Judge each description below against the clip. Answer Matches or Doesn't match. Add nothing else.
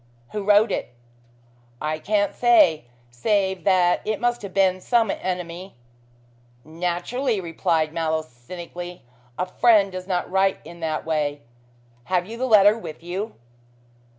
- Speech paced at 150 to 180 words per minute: Doesn't match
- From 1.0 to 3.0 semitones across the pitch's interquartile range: Doesn't match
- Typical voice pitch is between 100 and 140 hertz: Doesn't match